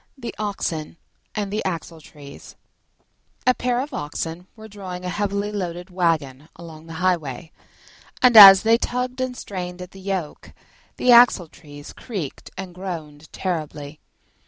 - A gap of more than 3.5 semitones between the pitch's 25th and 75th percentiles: Yes, average, 4.5 semitones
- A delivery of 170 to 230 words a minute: No, slow, 135 wpm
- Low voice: No, medium, 180 Hz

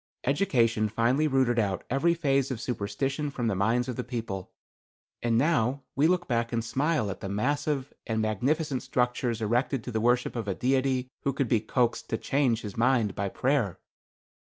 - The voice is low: Yes, low, 125 Hz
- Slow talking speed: No, average, 180 wpm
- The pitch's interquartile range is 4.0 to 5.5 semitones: No, average, 3.4 semitones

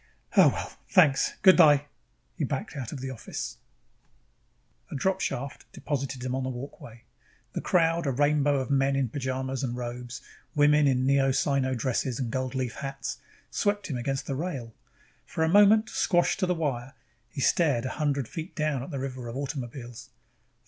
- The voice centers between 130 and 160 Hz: Yes, low, 135 Hz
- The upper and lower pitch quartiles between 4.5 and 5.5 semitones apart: No, average, 2.7 semitones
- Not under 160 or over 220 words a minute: Yes, average, 170 wpm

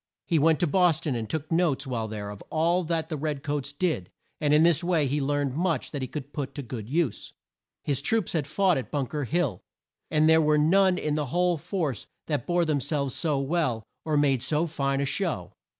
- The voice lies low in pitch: No, medium, 150 Hz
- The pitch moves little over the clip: No, average, 3.3 semitones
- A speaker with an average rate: No, fast, 220 wpm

